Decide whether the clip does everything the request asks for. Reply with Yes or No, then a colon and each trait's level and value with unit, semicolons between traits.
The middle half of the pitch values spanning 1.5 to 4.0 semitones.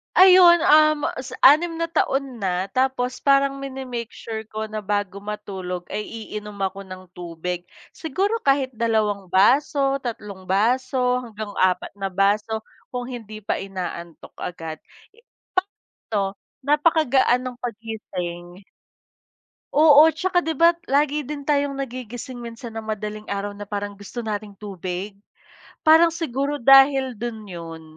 No: wide, 5.4 semitones